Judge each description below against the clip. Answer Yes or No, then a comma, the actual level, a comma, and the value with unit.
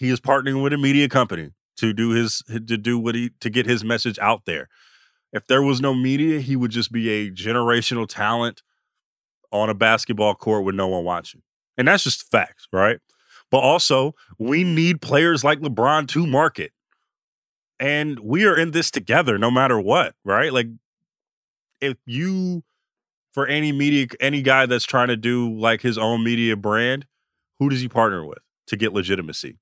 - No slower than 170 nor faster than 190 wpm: Yes, average, 180 wpm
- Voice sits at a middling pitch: No, low, 120 Hz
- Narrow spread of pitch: No, average, 3.6 semitones